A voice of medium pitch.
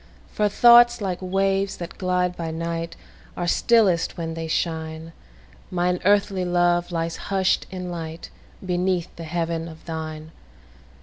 Yes: medium, 175 Hz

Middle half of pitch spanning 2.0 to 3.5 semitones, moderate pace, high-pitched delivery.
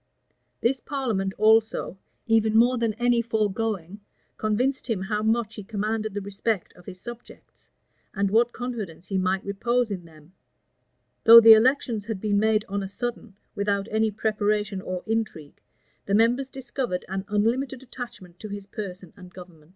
Yes: average, 3.1 semitones; average, 160 wpm; high, 215 Hz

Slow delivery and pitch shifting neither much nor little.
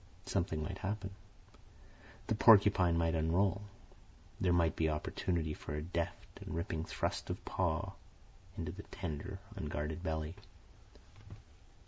Yes: slow, 120 wpm; average, 3.3 semitones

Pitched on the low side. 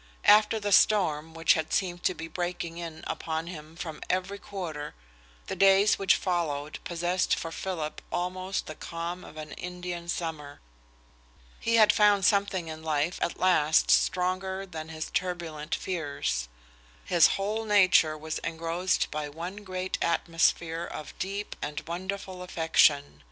No: medium, 175 Hz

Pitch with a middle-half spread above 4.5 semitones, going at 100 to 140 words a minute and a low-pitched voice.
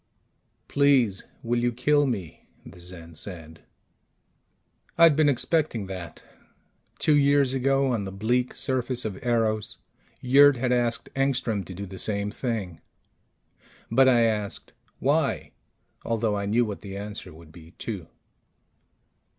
Yes: average, 5.0 semitones; slow, 135 wpm; low, 115 Hz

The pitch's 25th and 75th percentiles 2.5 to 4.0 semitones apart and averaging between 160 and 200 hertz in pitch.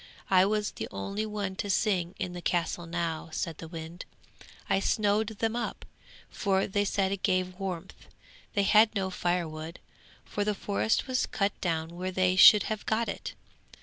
Yes: average, 3.0 semitones; high, 190 Hz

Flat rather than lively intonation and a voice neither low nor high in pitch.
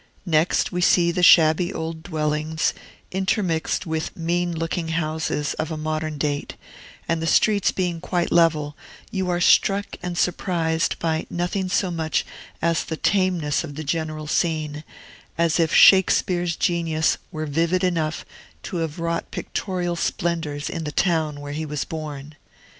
Yes: narrow, 2.1 semitones; medium, 165 Hz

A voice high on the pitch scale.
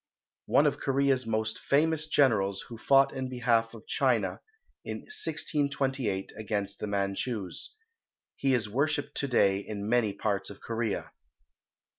No: low, 115 Hz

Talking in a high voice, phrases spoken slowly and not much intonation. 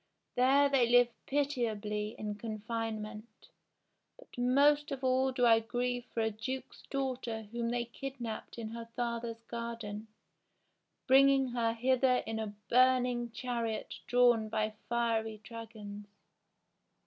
Yes: high, 235 Hz; slow, 130 wpm; narrow, 2.3 semitones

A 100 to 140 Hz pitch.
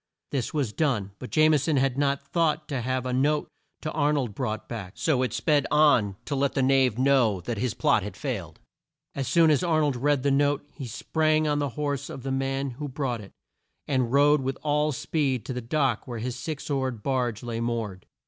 Yes: low, 135 Hz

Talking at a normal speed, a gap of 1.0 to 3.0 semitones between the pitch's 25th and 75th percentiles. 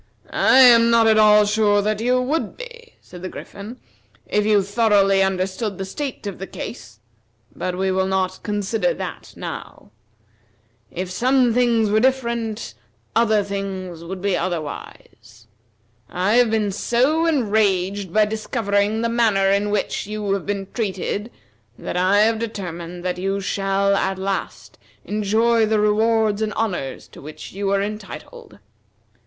Yes: average, 150 wpm; average, 2.7 semitones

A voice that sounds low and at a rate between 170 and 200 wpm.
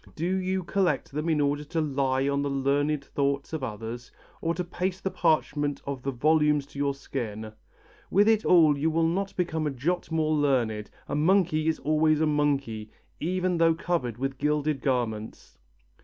No: medium, 150 Hz; average, 180 wpm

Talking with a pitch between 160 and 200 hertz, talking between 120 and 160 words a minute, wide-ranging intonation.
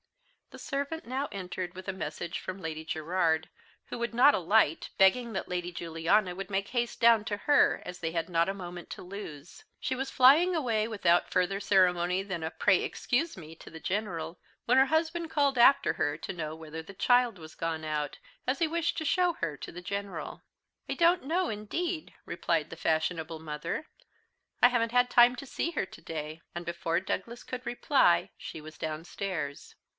No: high, 190 Hz; average, 190 wpm; wide, 7.0 semitones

